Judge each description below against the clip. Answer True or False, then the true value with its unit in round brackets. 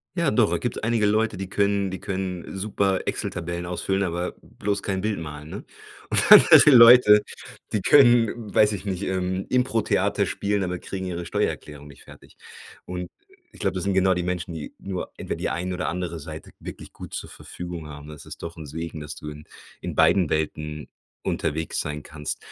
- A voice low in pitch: True (90 Hz)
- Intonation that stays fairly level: False (3.7 semitones)